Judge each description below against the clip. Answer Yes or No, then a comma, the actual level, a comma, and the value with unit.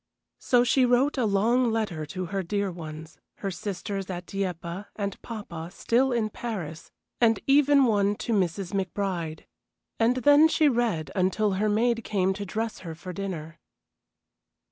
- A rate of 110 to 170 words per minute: Yes, average, 155 wpm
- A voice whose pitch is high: Yes, high, 200 Hz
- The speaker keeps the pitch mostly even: No, average, 4.5 semitones